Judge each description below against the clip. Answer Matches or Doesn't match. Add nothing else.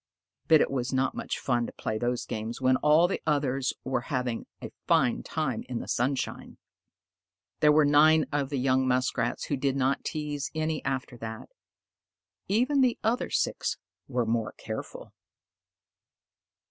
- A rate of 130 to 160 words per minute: Matches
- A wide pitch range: Doesn't match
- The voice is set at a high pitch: Doesn't match